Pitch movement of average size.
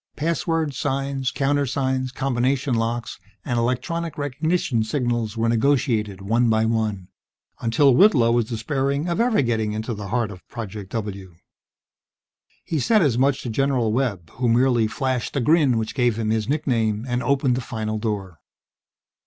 Yes: average, 3.8 semitones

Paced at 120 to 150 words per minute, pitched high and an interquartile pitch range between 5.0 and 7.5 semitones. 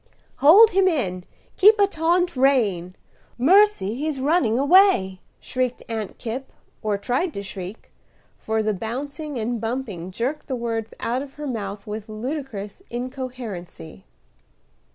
Yes: average, 140 wpm; high, 245 Hz; wide, 5.6 semitones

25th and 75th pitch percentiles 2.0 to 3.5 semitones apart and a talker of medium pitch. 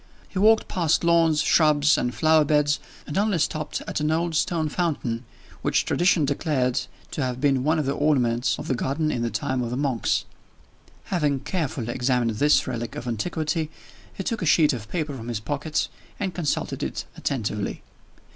No: average, 4.3 semitones; medium, 145 Hz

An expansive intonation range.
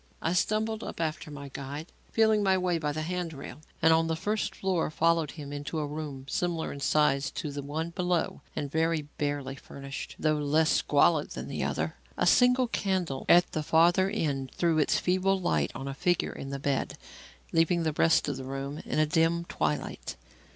No: average, 3.6 semitones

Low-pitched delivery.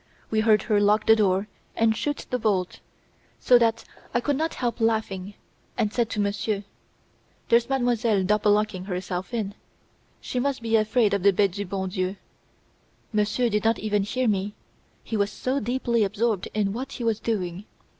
No: high, 215 Hz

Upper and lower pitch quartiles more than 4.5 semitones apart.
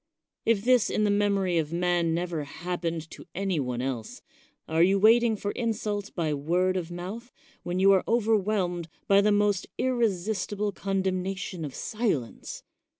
No: average, 3.4 semitones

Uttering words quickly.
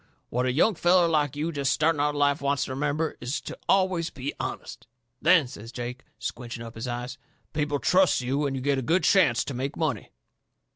Yes: fast, 210 wpm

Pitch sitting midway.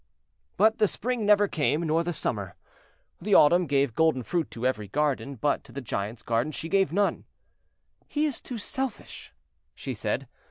Yes: medium, 160 Hz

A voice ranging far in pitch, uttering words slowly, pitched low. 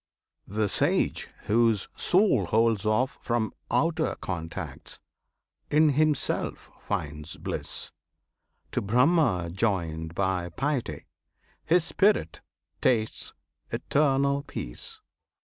Yes: wide, 7.9 semitones; slow, 90 wpm; low, 115 Hz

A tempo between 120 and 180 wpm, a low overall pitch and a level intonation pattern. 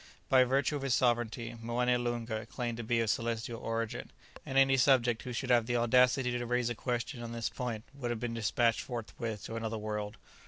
No: fast, 205 wpm; low, 120 Hz; narrow, 1.5 semitones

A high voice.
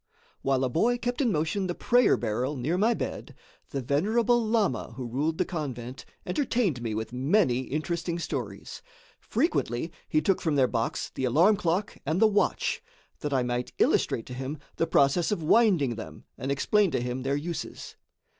No: medium, 155 Hz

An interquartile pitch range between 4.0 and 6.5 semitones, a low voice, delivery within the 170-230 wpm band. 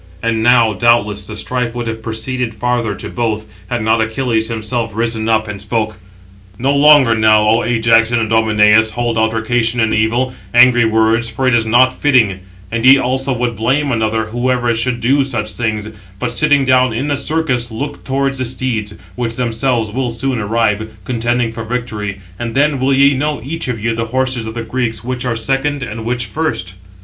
No: narrow, 2.4 semitones; low, 115 Hz; average, 190 wpm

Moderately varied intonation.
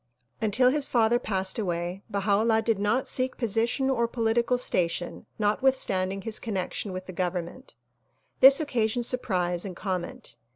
Yes: average, 4.4 semitones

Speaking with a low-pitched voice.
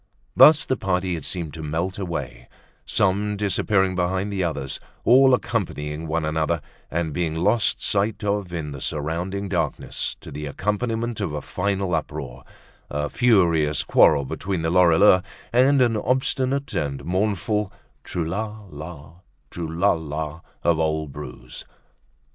Yes: very low, 90 Hz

